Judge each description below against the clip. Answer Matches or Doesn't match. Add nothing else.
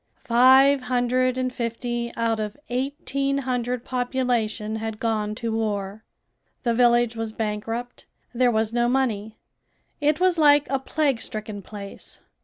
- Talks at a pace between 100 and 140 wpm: Matches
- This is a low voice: Doesn't match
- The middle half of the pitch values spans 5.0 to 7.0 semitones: Doesn't match